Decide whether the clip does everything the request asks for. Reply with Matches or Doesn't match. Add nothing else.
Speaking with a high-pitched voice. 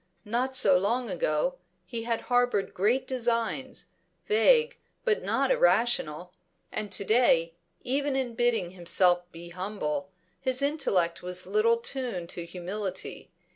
Matches